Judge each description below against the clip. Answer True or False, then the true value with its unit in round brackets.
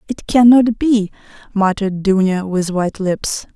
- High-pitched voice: True (205 Hz)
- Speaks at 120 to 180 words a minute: True (135 wpm)